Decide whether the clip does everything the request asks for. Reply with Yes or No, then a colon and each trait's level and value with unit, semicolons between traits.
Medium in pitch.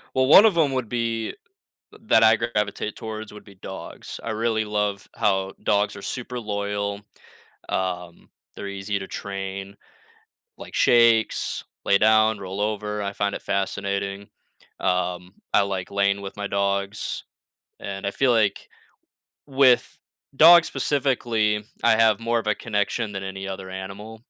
No: low, 105 Hz